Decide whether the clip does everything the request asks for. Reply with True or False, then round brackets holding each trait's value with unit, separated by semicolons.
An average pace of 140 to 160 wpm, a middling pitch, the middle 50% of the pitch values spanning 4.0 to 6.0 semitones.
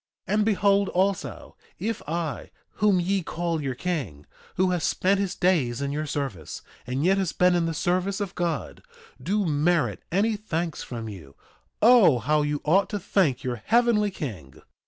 False (175 wpm; 175 Hz; 5.6 semitones)